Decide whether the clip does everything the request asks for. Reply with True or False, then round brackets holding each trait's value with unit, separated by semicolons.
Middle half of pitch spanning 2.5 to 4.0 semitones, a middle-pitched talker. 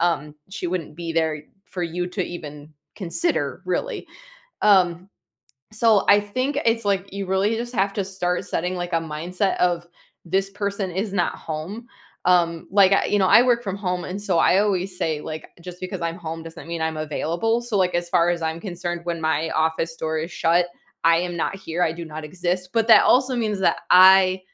True (3.2 semitones; 180 Hz)